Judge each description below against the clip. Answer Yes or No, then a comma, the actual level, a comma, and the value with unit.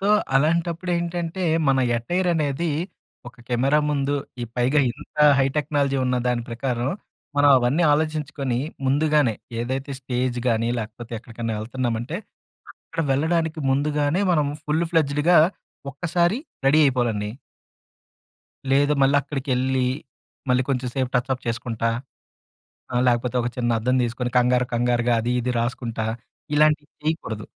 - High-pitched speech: No, low, 135 Hz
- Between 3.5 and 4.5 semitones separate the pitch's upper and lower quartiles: Yes, average, 3.8 semitones